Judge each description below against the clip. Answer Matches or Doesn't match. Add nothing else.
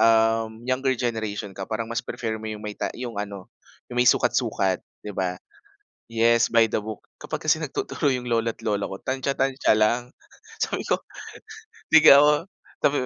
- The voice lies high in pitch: Doesn't match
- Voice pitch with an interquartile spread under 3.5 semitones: Matches